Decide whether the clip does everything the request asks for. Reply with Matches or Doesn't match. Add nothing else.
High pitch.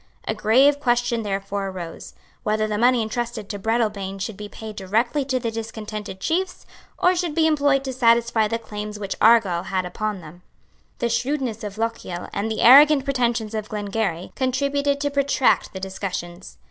Matches